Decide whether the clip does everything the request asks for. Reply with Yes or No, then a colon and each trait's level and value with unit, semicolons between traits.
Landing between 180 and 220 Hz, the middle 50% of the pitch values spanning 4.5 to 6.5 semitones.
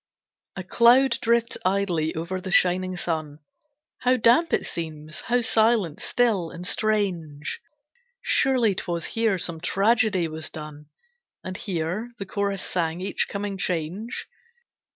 Yes: medium, 185 Hz; average, 5.1 semitones